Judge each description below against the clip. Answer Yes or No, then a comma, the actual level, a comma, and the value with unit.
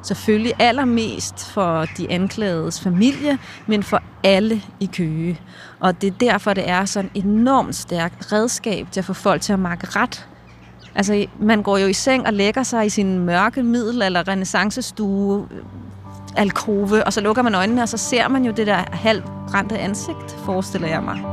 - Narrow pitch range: No, average, 3.5 semitones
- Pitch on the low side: No, high, 200 Hz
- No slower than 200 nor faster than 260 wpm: No, average, 175 wpm